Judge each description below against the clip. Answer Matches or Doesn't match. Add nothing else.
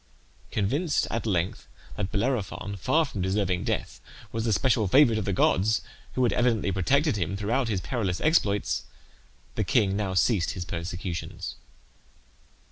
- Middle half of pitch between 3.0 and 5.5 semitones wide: Matches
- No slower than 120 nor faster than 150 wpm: Matches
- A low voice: Matches